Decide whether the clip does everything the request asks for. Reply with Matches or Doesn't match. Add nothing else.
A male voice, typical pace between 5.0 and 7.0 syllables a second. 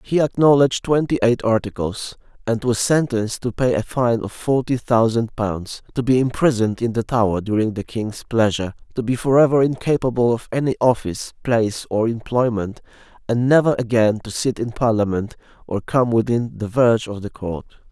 Matches